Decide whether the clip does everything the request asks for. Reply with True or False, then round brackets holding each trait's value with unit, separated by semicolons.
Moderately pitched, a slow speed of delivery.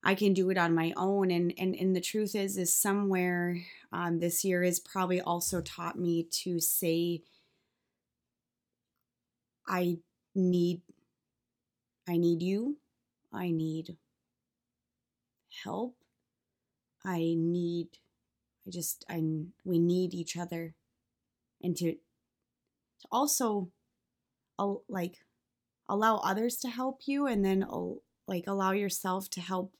True (180 Hz; 125 wpm)